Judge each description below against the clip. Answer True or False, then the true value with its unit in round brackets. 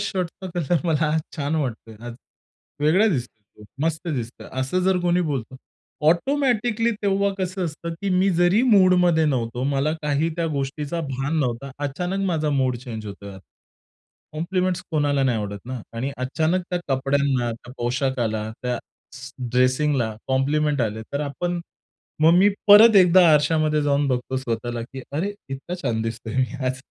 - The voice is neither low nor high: True (145 Hz)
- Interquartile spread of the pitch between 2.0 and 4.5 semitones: False (5.6 semitones)